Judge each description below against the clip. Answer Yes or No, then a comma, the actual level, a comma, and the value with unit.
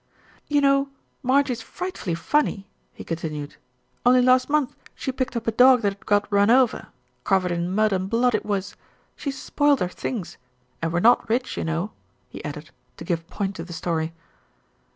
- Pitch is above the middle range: Yes, high, 215 Hz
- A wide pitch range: Yes, wide, 6.0 semitones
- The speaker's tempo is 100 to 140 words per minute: No, average, 185 wpm